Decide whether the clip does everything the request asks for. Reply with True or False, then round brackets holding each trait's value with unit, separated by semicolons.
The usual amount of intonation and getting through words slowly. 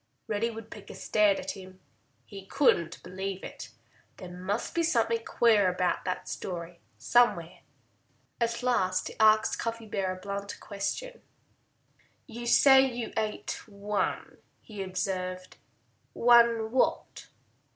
True (3.9 semitones; 120 wpm)